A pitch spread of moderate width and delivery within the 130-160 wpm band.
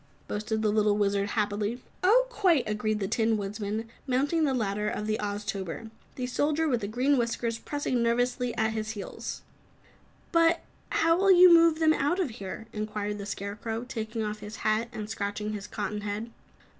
No: average, 3.9 semitones; average, 170 wpm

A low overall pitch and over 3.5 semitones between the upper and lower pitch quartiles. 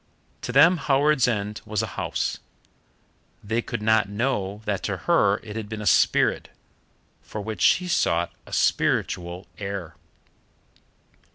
No: low, 105 Hz; average, 3.0 semitones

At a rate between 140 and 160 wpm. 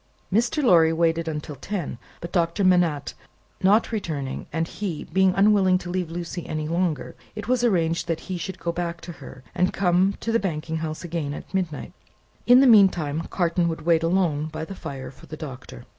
No: average, 190 wpm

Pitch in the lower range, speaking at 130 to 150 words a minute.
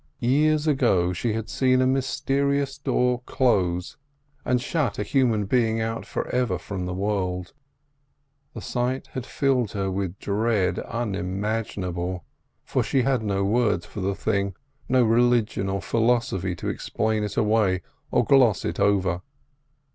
Yes: low, 110 Hz; average, 145 wpm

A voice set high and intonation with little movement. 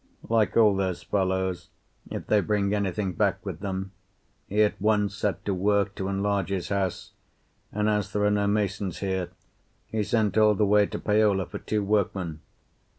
No: low, 100 Hz; narrow, 1.5 semitones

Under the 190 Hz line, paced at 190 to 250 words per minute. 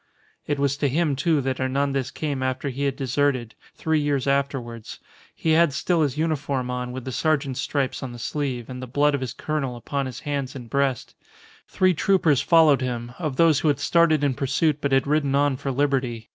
Yes: medium, 140 Hz; fast, 205 wpm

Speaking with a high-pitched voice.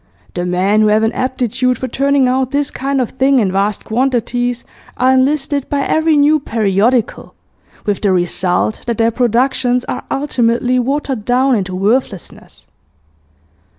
Yes: high, 245 Hz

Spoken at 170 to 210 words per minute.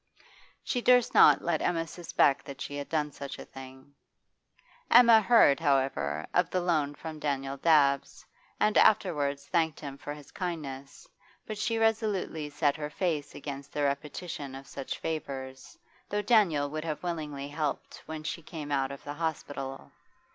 No: average, 160 wpm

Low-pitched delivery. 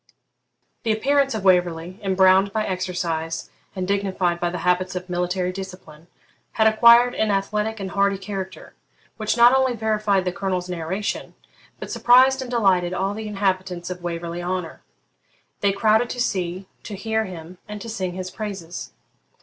No: high, 190 Hz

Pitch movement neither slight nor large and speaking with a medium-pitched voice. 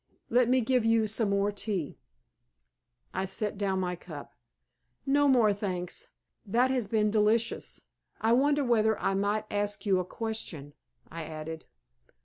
No: average, 3.3 semitones; high, 210 Hz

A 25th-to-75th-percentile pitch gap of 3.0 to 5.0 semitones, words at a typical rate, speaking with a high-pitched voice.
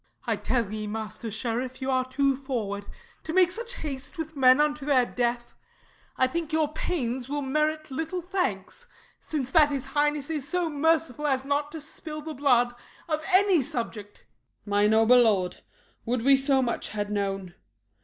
Yes: average, 4.4 semitones; average, 175 wpm; very high, 270 Hz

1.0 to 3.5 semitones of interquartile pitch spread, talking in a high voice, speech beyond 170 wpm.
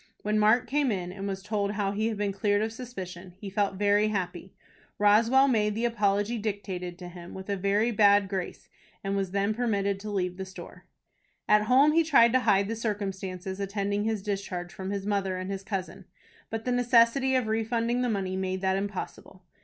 Yes: narrow, 2.6 semitones; high, 205 Hz; average, 200 wpm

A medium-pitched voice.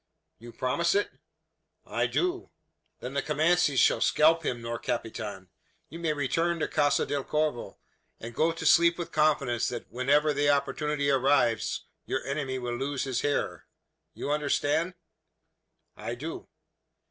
Yes: medium, 145 Hz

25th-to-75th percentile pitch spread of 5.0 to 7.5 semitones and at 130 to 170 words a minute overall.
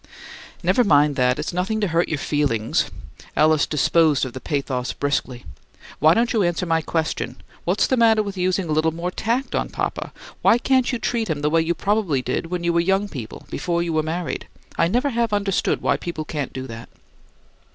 No: wide, 5.4 semitones; fast, 205 wpm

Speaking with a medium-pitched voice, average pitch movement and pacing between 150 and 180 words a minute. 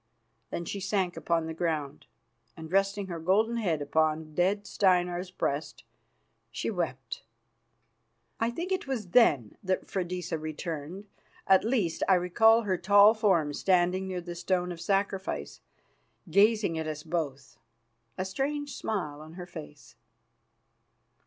No: medium, 180 Hz; average, 3.9 semitones; slow, 135 wpm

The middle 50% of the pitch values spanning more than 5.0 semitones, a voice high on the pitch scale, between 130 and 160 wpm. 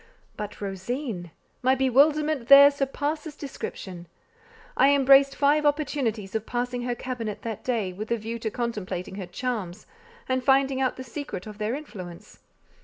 No: average, 4.7 semitones; high, 245 Hz; average, 150 wpm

